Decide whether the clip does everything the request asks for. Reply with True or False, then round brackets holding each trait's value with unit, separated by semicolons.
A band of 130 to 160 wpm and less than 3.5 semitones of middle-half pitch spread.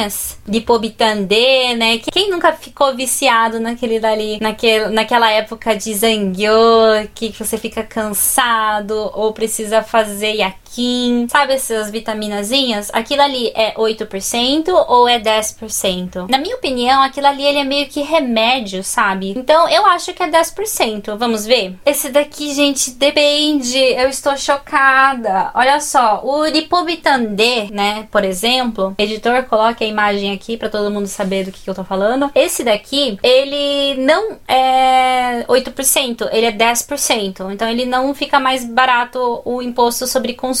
False (145 wpm; 4.1 semitones)